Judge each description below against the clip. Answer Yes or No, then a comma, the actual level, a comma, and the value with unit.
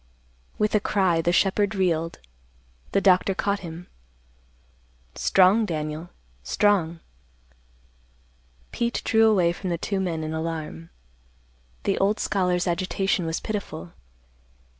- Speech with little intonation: No, average, 3.5 semitones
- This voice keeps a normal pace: No, slow, 115 wpm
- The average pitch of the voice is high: No, medium, 180 Hz